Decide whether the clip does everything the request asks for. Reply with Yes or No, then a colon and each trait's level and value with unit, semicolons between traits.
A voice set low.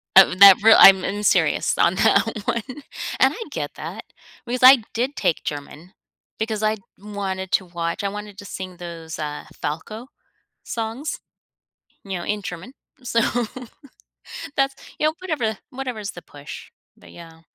No: high, 205 Hz